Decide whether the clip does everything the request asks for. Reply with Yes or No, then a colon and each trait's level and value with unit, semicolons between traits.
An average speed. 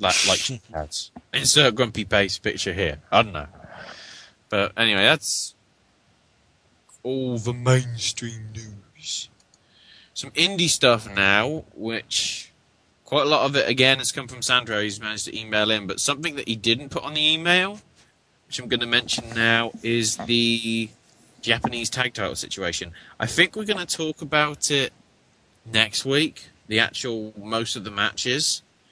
Yes: average, 155 wpm